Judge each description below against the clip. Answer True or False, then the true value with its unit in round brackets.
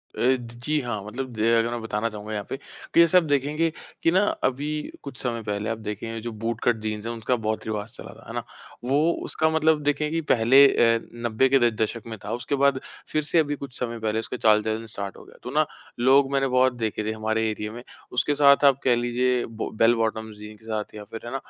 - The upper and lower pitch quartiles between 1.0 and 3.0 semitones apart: False (3.8 semitones)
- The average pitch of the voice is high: False (120 Hz)